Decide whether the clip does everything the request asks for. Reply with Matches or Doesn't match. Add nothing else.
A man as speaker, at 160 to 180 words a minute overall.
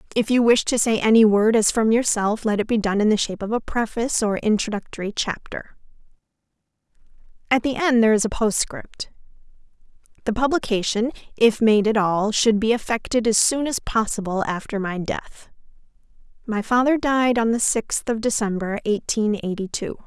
Doesn't match